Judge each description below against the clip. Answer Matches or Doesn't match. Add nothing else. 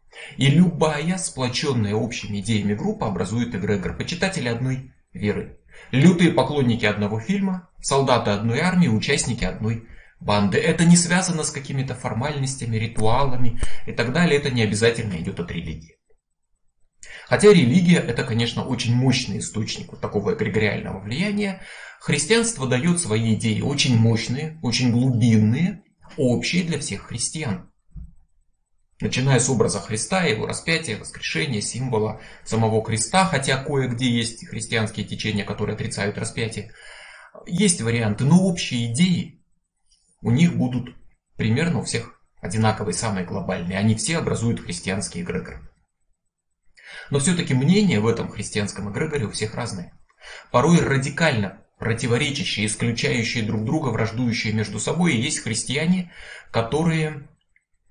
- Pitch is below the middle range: Matches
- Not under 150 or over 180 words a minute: Doesn't match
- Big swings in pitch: Matches